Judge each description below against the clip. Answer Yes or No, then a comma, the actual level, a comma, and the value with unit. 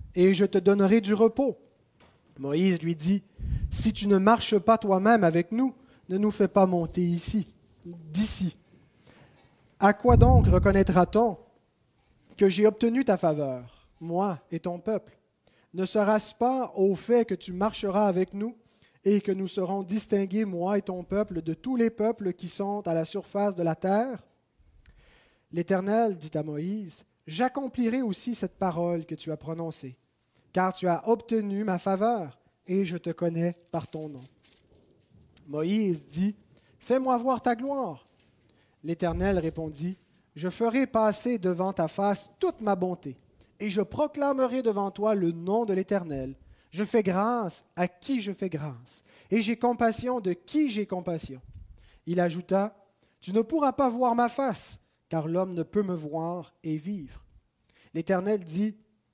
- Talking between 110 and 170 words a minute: Yes, average, 155 wpm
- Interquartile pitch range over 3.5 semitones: Yes, average, 4.2 semitones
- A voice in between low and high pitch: No, high, 195 Hz